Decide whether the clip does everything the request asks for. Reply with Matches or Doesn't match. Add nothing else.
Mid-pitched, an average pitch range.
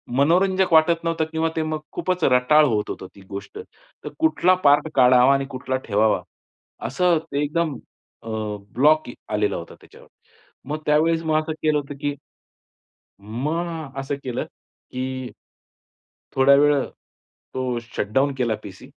Matches